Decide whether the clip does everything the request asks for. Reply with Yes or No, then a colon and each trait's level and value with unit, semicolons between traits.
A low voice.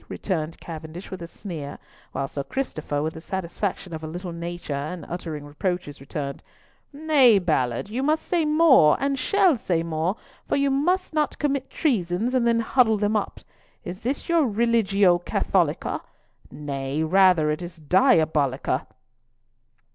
No: medium, 180 Hz